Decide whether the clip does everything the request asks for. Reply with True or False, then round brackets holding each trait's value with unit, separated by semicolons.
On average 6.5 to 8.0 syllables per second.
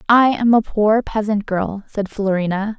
False (4.3 syllables/s)